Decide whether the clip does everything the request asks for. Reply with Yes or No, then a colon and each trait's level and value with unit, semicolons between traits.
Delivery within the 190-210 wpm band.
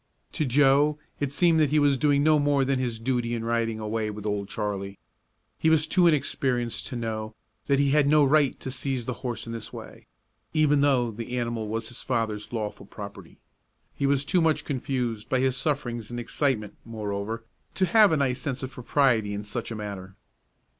Yes: average, 195 wpm